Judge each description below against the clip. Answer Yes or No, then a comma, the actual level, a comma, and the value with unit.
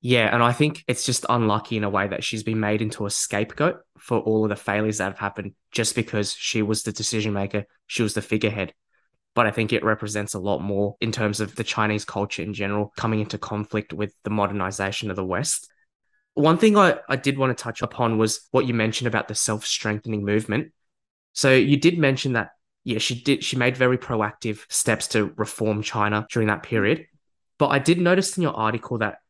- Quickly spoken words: Yes, fast, 215 wpm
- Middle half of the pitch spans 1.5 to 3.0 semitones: Yes, average, 2.7 semitones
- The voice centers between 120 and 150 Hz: No, low, 110 Hz